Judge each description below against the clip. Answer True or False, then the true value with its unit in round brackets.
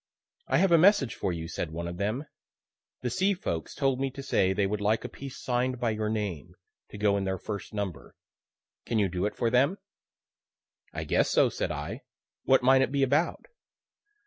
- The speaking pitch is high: False (110 Hz)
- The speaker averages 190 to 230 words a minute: True (200 wpm)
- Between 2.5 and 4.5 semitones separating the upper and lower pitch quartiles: False (5.6 semitones)